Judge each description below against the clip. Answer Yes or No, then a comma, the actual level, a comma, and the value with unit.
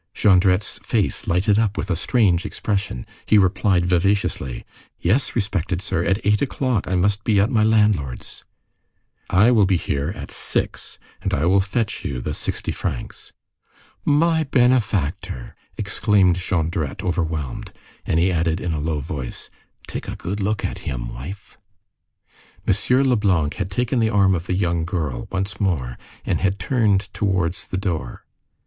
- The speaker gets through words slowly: No, average, 155 wpm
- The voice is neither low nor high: No, very low, 95 Hz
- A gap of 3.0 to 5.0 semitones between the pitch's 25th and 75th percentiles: Yes, average, 3.8 semitones